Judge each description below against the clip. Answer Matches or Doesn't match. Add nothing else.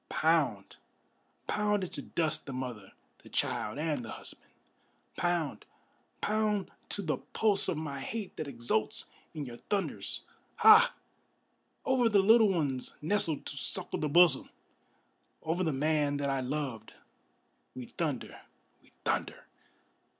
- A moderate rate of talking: Doesn't match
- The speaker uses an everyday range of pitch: Doesn't match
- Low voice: Doesn't match